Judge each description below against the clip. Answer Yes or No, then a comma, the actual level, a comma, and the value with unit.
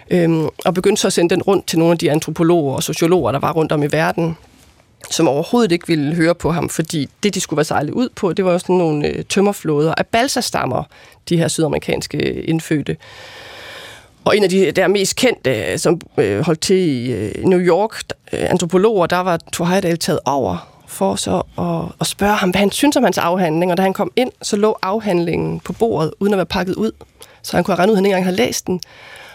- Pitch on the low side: No, medium, 175 Hz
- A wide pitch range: No, average, 3.3 semitones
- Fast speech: No, average, 215 wpm